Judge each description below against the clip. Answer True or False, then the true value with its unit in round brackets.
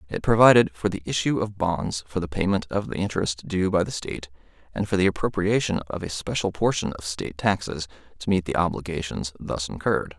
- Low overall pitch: True (90 Hz)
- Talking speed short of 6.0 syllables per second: True (5.8 syllables/s)